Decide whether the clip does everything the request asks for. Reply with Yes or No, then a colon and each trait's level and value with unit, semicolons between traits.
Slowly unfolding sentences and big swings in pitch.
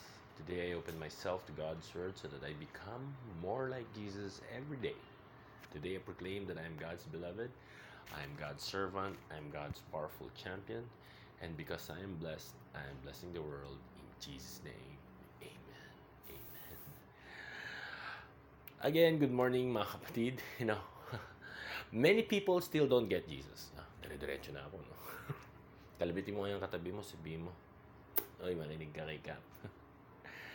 Yes: slow, 120 wpm; wide, 6.3 semitones